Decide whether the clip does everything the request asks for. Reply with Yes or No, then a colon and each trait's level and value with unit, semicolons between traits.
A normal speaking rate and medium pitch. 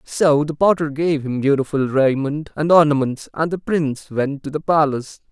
Yes: average, 180 wpm; medium, 145 Hz